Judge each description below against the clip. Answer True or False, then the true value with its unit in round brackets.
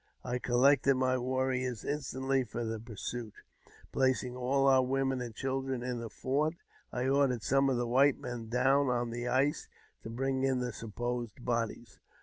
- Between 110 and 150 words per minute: False (165 wpm)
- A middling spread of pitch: False (1.8 semitones)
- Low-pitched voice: True (125 Hz)